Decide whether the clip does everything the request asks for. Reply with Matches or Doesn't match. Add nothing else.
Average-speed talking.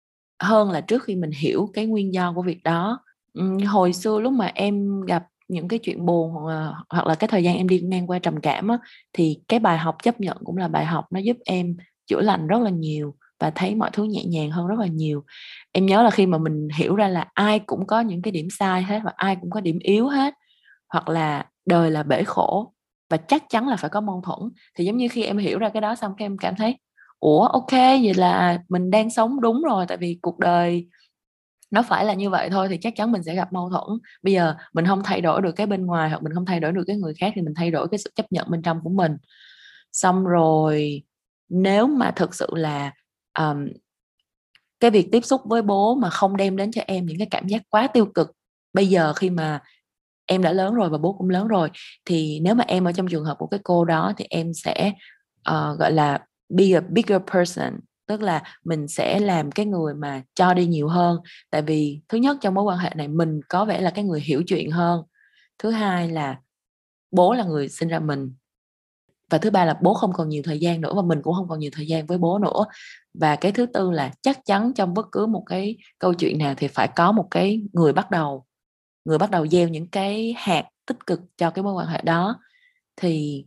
Matches